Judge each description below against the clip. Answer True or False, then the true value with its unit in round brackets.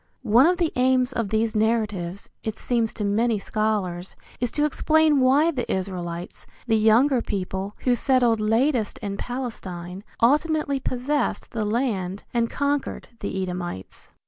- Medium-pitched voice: False (225 Hz)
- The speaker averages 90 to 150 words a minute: True (145 wpm)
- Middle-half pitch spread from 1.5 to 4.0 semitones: False (4.6 semitones)